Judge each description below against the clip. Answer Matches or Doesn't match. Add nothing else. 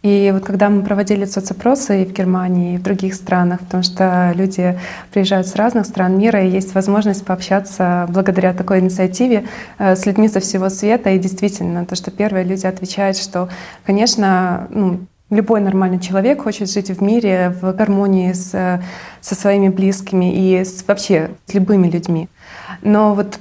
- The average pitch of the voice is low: Doesn't match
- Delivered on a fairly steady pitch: Matches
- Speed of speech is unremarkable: Doesn't match